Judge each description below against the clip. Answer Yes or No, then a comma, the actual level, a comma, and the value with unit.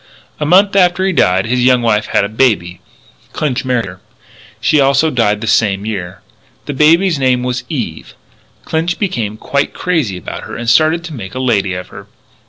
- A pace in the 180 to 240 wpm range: Yes, average, 190 wpm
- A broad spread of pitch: Yes, wide, 6.9 semitones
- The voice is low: Yes, low, 125 Hz